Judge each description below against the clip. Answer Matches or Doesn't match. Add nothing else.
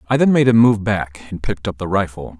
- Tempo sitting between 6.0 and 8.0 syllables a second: Matches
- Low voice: Matches